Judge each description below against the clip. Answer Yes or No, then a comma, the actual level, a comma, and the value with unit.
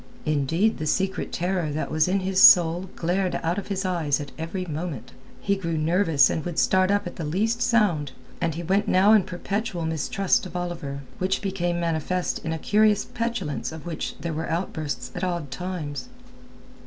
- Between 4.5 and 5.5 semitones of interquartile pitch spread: No, average, 3.3 semitones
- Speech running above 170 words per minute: Yes, average, 190 wpm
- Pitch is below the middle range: No, medium, 175 Hz